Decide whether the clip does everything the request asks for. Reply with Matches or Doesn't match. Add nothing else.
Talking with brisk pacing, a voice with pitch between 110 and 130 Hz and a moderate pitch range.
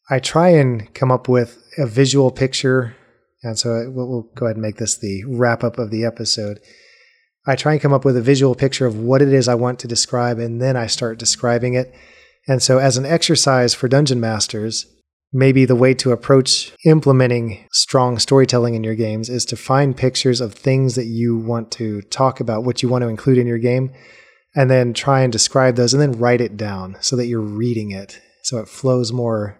Doesn't match